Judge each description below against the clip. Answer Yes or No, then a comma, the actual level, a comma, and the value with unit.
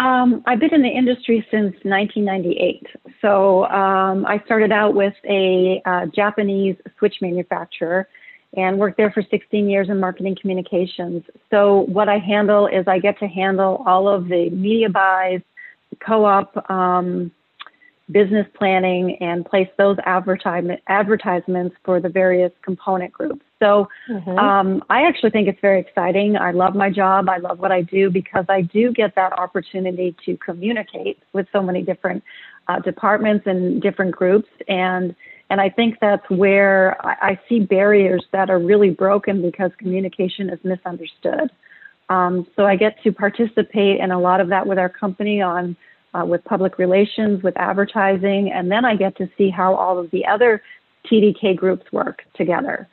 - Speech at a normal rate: Yes, average, 165 wpm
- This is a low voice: No, high, 195 Hz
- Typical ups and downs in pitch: No, narrow, 2.1 semitones